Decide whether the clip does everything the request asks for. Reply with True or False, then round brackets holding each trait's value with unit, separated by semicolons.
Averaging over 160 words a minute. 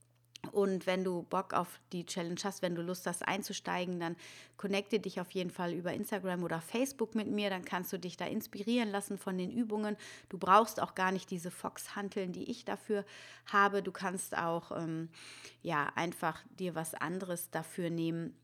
True (185 wpm)